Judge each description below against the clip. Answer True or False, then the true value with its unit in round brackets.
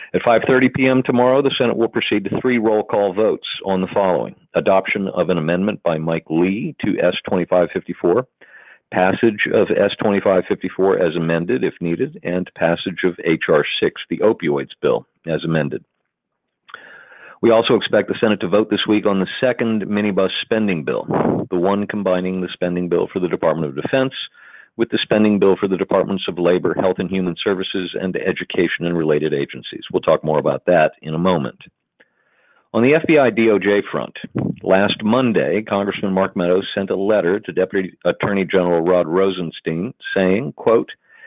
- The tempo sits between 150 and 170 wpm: True (165 wpm)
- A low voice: True (95 Hz)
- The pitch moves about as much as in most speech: True (3.2 semitones)